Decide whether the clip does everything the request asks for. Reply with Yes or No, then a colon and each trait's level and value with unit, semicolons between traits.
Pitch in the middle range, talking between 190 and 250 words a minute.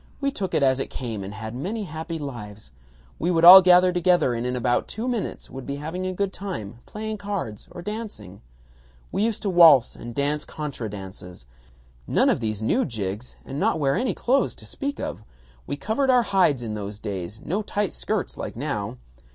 Yes: medium, 150 Hz; average, 195 wpm